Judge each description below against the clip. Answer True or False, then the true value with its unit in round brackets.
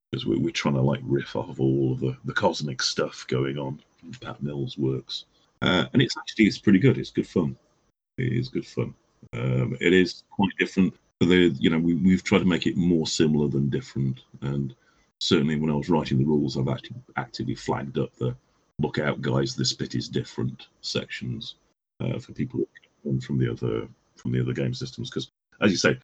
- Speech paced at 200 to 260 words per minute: True (205 wpm)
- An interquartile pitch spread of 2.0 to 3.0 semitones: True (2.7 semitones)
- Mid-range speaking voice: False (70 Hz)